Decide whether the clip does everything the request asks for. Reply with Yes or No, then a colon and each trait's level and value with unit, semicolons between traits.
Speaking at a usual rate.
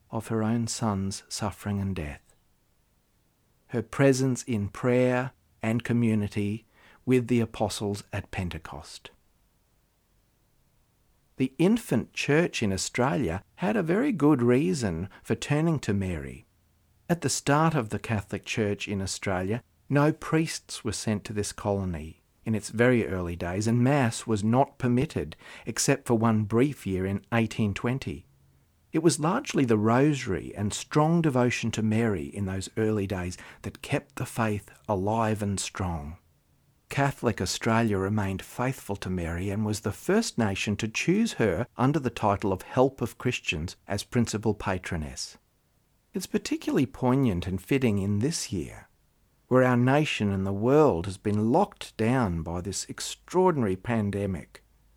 Yes: average, 145 wpm